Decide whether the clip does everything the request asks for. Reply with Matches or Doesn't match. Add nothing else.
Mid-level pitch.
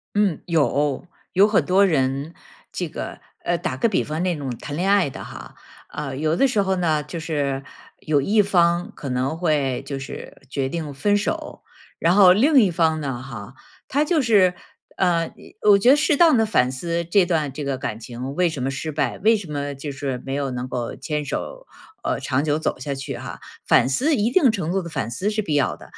Matches